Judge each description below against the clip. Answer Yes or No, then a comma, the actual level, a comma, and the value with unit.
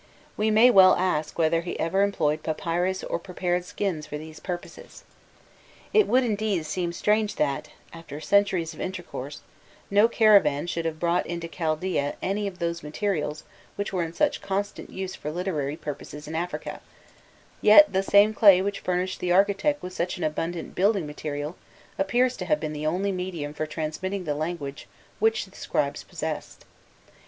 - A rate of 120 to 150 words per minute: No, average, 165 wpm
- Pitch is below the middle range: No, medium, 180 Hz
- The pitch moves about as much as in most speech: Yes, average, 4.1 semitones